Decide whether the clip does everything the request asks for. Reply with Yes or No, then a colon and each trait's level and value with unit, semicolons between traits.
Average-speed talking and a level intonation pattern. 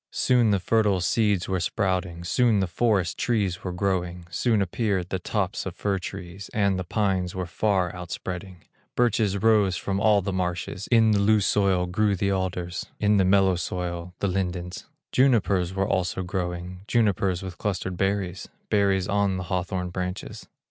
Yes: average, 165 wpm; narrow, 2.2 semitones